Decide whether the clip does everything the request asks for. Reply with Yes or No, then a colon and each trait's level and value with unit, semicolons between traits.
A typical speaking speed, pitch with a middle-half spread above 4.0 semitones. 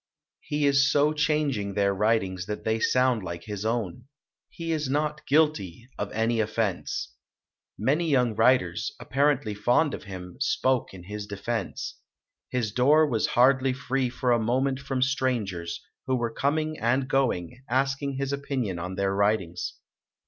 Yes: average, 160 wpm; average, 5.0 semitones